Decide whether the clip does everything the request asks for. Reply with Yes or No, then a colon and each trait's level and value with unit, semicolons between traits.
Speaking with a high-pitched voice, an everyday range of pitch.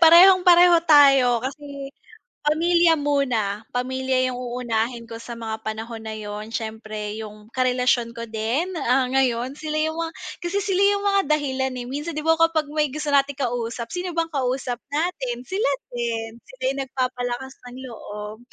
Yes: very high, 260 Hz; average, 4.7 semitones